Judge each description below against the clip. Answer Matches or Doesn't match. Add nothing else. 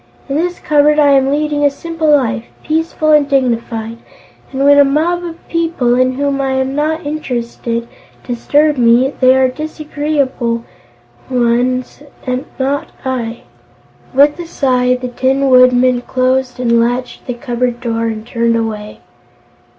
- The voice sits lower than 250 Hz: Doesn't match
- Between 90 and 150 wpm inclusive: Matches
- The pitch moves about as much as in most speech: Matches